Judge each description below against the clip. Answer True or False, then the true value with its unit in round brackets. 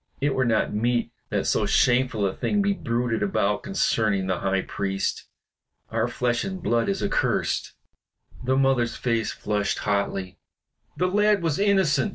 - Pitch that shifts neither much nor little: False (5.8 semitones)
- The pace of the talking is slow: False (155 wpm)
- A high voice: False (120 Hz)